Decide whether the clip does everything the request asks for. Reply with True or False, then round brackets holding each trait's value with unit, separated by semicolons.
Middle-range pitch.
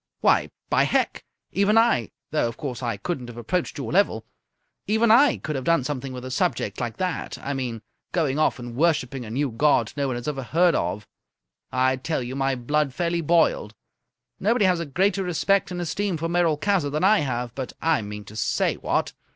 True (145 Hz)